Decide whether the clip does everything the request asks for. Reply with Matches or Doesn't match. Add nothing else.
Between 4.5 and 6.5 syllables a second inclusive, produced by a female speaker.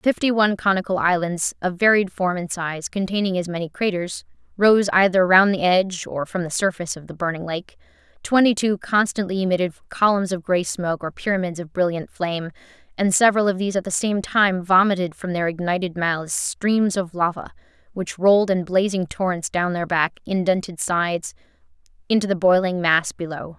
Matches